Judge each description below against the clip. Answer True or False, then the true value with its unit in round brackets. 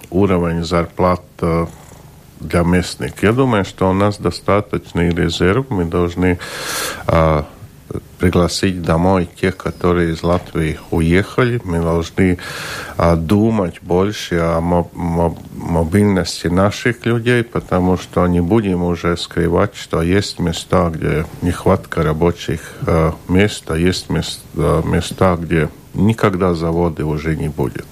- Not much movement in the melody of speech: True (2.1 semitones)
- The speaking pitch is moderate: False (90 Hz)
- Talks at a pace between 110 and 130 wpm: True (115 wpm)